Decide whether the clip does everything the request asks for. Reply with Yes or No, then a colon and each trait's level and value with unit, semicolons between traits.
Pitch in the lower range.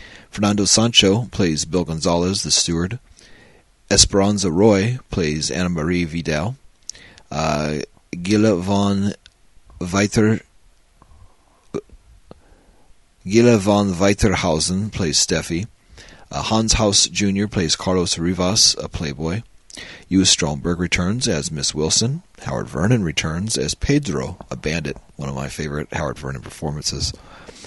Yes: very low, 95 Hz